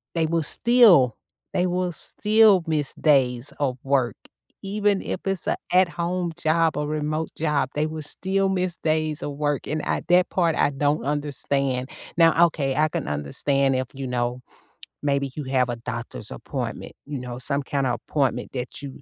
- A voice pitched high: No, medium, 150 Hz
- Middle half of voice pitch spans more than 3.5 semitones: Yes, average, 4.0 semitones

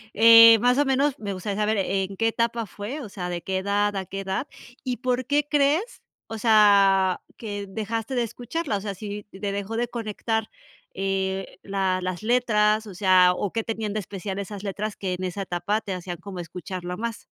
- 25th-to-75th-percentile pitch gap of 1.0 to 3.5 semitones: Yes, average, 3.0 semitones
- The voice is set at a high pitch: Yes, high, 205 Hz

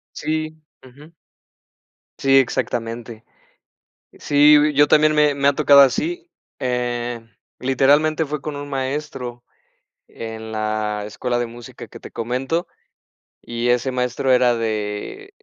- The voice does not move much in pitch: No, average, 3.7 semitones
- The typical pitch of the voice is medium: No, low, 130 Hz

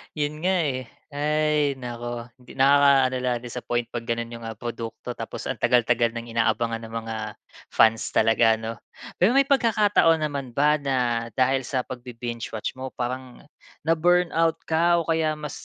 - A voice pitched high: No, low, 130 Hz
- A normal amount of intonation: Yes, average, 4.4 semitones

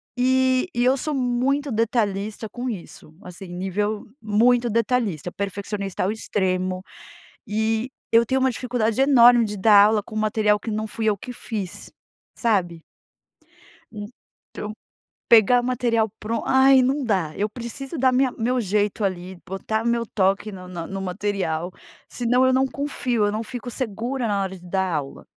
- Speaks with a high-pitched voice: Yes, high, 220 Hz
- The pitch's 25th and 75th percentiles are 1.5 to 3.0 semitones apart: No, average, 3.9 semitones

